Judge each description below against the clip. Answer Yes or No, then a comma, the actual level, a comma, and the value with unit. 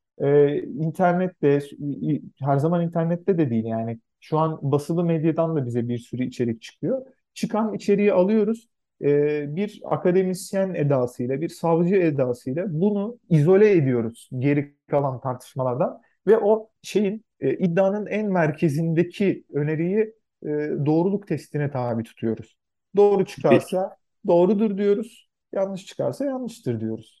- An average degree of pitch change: No, wide, 5.8 semitones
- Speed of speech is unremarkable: Yes, average, 120 wpm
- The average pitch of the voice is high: No, medium, 165 Hz